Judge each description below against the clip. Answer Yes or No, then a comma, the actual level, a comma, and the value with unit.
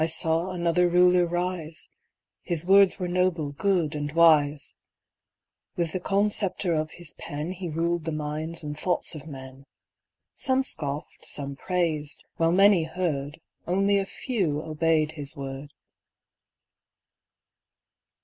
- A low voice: No, medium, 165 Hz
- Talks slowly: Yes, slow, 130 wpm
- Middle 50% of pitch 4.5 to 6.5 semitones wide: No, average, 3.2 semitones